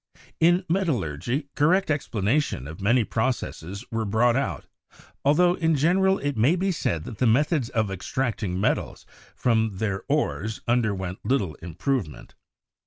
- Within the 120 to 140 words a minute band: Yes, slow, 135 wpm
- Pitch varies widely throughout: Yes, wide, 7.1 semitones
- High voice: No, low, 120 Hz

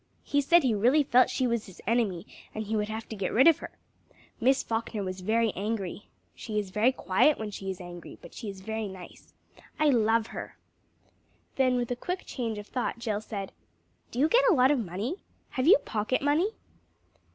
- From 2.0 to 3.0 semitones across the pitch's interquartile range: No, average, 4.0 semitones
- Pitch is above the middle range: Yes, high, 225 Hz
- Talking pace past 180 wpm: Yes, average, 200 wpm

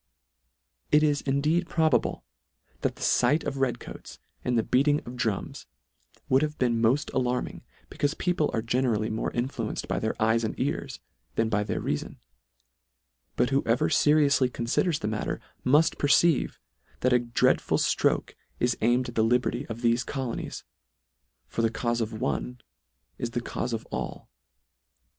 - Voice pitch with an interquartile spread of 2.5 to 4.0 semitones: Yes, average, 3.5 semitones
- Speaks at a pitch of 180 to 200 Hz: No, low, 125 Hz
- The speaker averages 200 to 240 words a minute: No, average, 155 wpm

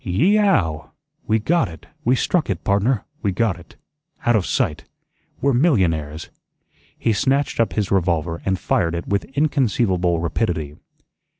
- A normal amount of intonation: No, wide, 6.6 semitones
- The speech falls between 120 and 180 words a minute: Yes, average, 155 wpm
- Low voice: Yes, low, 100 Hz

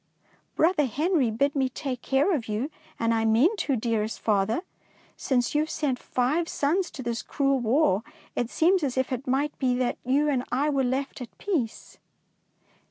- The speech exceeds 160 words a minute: Yes, average, 180 wpm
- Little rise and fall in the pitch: No, average, 3.6 semitones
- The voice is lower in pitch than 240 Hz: No, very high, 265 Hz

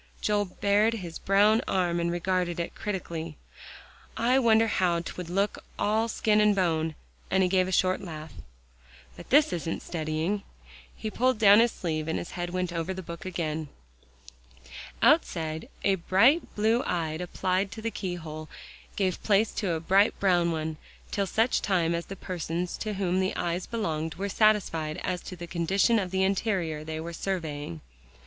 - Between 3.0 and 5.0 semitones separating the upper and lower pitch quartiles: Yes, average, 3.6 semitones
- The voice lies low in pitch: No, medium, 185 Hz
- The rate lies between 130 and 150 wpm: No, average, 170 wpm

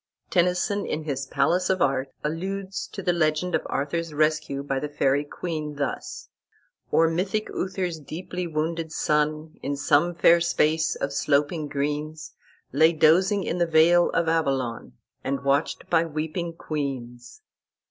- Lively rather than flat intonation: No, average, 3.0 semitones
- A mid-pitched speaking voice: Yes, medium, 155 Hz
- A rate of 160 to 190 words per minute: No, average, 145 wpm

